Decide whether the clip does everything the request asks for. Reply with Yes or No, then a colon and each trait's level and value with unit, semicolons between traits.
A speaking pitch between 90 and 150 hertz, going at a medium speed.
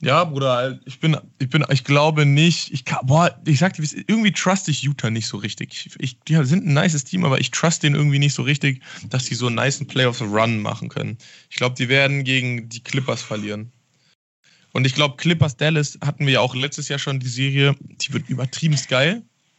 No: medium, 140 Hz; fast, 205 wpm